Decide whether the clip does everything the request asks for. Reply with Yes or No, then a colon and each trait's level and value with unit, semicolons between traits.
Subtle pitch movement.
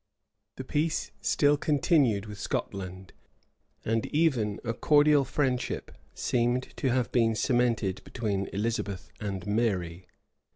No: average, 4.7 semitones